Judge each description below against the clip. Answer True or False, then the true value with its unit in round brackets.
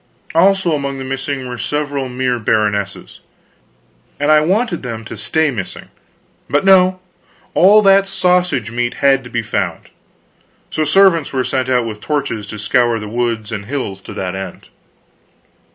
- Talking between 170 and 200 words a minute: False (155 wpm)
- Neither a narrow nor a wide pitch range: False (5.8 semitones)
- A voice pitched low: True (130 Hz)